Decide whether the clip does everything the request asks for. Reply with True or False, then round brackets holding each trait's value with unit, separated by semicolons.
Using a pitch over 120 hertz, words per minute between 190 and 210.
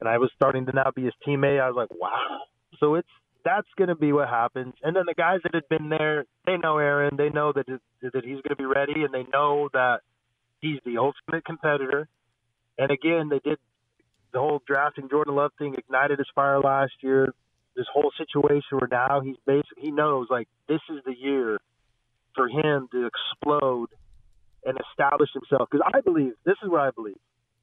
True (140 Hz; 205 wpm)